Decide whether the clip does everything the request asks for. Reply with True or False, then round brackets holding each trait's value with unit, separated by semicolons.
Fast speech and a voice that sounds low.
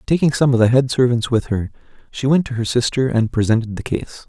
True (240 wpm; 125 Hz)